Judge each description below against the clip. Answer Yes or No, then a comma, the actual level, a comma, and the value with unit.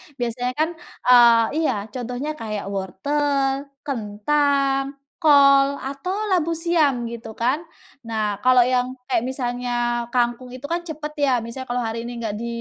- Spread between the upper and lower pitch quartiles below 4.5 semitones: Yes, average, 3.4 semitones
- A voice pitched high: Yes, very high, 255 Hz